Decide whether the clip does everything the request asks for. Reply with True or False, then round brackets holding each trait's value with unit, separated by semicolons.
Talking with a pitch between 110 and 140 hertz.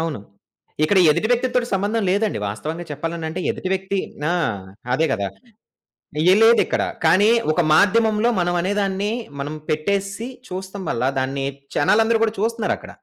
False (190 Hz)